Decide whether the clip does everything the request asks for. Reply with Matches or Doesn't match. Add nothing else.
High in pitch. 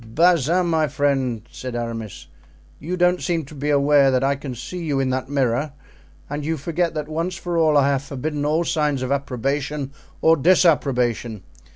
Doesn't match